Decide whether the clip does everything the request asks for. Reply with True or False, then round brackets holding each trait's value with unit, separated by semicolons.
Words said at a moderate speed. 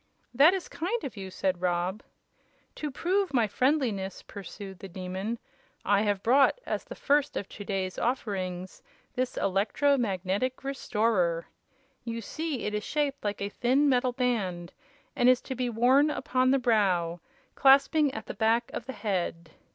True (160 wpm)